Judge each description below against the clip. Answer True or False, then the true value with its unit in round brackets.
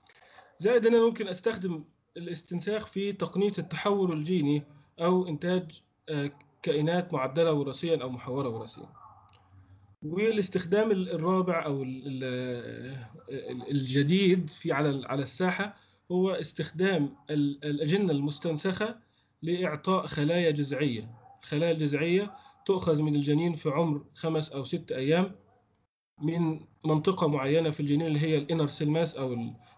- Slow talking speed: False (110 wpm)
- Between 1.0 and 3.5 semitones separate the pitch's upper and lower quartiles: False (4.1 semitones)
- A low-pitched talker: False (160 Hz)